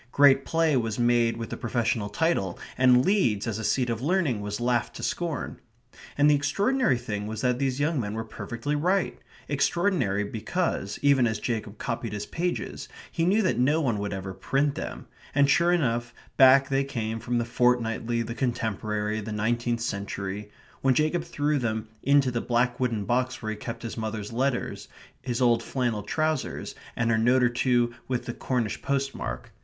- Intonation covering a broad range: No, average, 3.9 semitones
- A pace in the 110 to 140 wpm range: No, average, 180 wpm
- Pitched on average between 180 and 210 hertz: No, low, 120 Hz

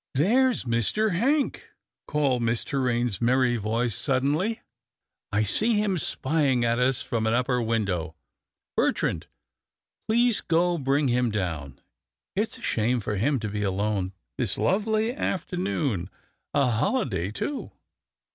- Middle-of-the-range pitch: No, low, 125 Hz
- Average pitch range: No, wide, 8.3 semitones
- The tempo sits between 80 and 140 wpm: Yes, slow, 135 wpm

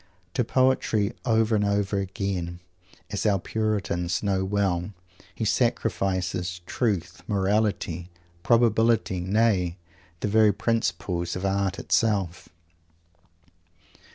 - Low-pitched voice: Yes, low, 100 Hz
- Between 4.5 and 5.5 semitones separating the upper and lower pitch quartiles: No, average, 3.3 semitones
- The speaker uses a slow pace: Yes, slow, 100 wpm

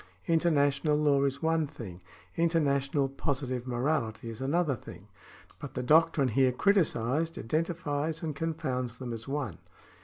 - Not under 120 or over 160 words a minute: Yes, average, 140 wpm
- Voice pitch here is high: No, medium, 140 Hz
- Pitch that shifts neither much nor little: Yes, average, 4.1 semitones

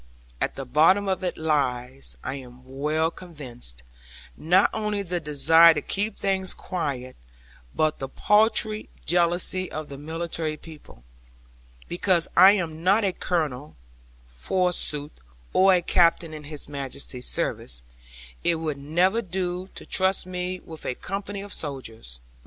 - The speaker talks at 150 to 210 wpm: No, average, 140 wpm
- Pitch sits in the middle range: Yes, medium, 165 Hz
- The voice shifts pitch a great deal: No, average, 4.6 semitones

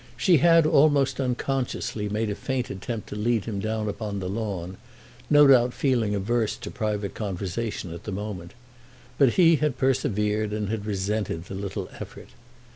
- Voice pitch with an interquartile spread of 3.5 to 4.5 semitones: Yes, average, 4.2 semitones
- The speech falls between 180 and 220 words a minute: No, average, 165 wpm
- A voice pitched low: Yes, low, 110 Hz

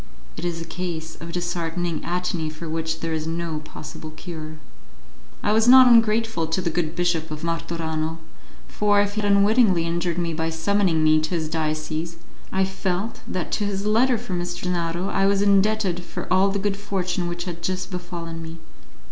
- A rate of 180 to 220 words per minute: Yes, average, 185 wpm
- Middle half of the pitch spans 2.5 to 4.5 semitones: Yes, average, 3.2 semitones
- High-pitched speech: No, medium, 175 Hz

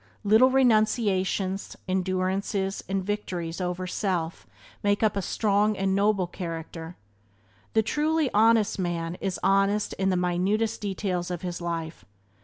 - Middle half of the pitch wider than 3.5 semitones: No, average, 2.8 semitones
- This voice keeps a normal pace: No, slow, 130 wpm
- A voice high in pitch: Yes, high, 195 Hz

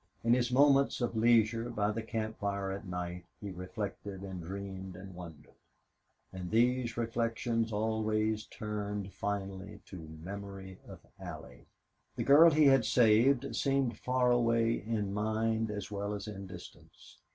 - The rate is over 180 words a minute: No, average, 145 wpm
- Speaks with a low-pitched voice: Yes, low, 105 Hz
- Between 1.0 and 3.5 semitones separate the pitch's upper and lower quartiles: Yes, average, 3.1 semitones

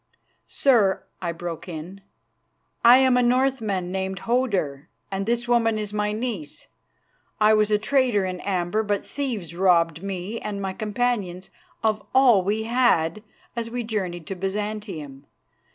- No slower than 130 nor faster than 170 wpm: Yes, average, 145 wpm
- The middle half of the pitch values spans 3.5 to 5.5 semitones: Yes, average, 4.2 semitones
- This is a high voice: Yes, high, 210 Hz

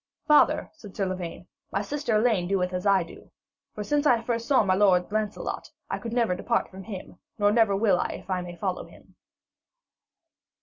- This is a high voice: Yes, high, 205 Hz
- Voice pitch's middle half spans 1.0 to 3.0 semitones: No, average, 3.8 semitones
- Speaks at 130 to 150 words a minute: No, average, 185 wpm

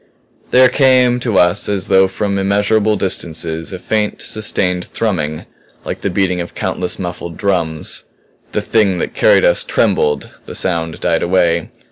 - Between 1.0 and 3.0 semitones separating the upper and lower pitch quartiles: No, average, 3.5 semitones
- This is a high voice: No, very low, 95 Hz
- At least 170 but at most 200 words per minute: No, average, 150 wpm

